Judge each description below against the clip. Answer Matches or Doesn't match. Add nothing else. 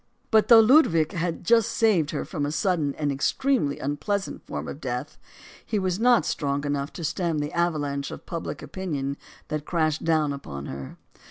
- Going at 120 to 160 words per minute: Doesn't match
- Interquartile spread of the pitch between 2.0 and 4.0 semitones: Doesn't match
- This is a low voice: Doesn't match